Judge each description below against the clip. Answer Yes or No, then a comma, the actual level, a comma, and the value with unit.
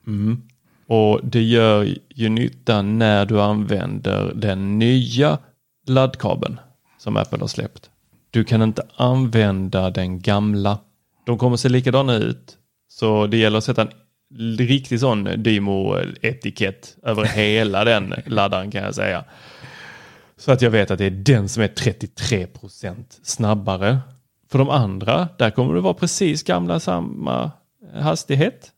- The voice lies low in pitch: Yes, low, 110 Hz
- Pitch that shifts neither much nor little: Yes, average, 3.5 semitones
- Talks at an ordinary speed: Yes, average, 140 wpm